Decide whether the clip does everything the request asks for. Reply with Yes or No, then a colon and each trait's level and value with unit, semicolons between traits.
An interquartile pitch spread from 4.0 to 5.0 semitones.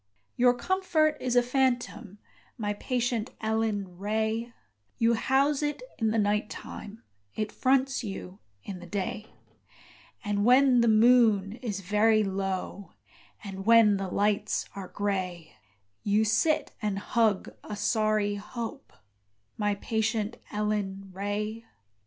No: average, 2.8 semitones